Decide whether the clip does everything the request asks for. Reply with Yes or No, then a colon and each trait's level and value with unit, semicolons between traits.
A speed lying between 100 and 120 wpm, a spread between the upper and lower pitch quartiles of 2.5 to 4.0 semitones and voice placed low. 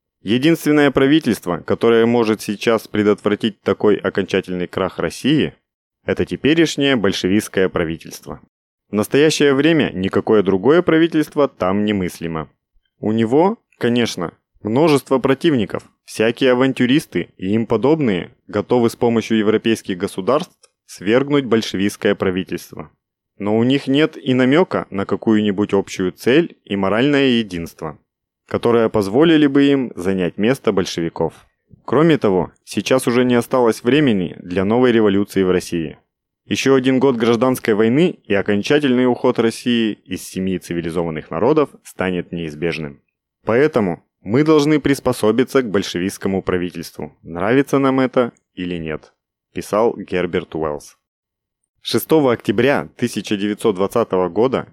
No: average, 115 wpm; wide, 5.4 semitones; low, 110 Hz